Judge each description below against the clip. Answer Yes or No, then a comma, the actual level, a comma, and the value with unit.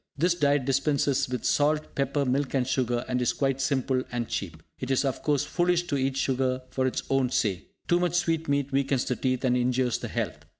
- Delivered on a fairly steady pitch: Yes, narrow, 2.0 semitones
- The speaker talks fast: Yes, fast, 210 wpm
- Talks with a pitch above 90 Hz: Yes, low, 135 Hz